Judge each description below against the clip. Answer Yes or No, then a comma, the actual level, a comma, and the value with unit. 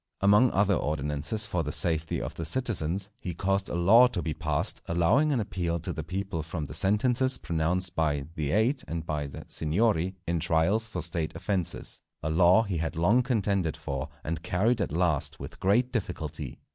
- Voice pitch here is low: Yes, very low, 90 Hz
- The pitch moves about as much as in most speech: Yes, average, 4.5 semitones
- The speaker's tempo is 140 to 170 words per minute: No, average, 185 wpm